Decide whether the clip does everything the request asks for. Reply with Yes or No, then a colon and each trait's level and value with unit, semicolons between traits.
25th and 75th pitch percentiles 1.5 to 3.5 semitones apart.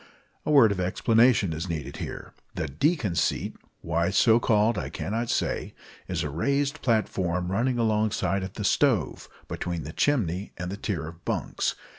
No: average, 5.0 semitones